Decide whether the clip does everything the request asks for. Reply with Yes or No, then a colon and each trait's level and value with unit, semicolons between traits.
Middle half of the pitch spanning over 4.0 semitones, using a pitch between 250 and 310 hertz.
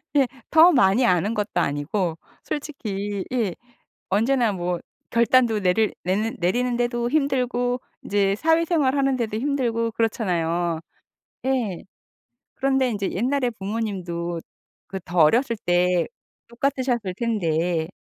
No: wide, 5.6 semitones; high, 225 Hz